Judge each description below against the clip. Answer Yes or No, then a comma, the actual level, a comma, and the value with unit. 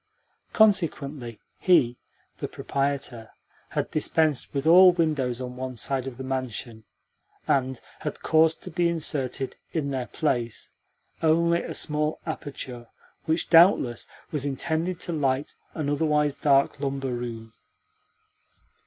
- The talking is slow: Yes, slow, 125 wpm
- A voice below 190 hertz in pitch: Yes, medium, 140 Hz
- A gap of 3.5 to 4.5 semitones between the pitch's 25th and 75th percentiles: Yes, average, 3.8 semitones